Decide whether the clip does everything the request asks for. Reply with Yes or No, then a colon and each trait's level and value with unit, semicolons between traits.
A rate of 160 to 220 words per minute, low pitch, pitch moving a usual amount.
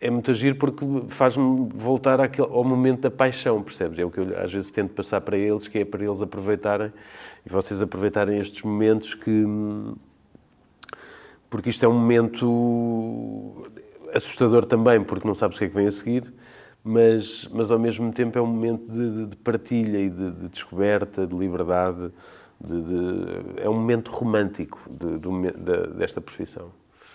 Yes: average, 175 wpm; low, 115 Hz; average, 3.1 semitones